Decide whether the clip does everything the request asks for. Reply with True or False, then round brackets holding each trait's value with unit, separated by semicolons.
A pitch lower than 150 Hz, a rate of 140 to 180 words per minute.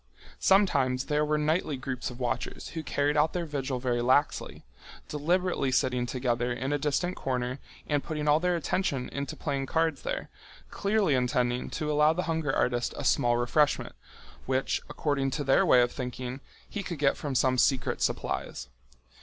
True (140 Hz; 170 wpm)